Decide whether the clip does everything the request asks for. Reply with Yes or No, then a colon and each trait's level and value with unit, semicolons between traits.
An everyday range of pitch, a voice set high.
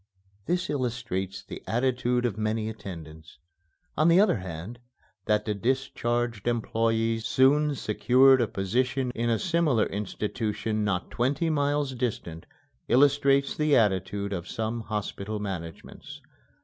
No: average, 4.2 semitones; low, 115 Hz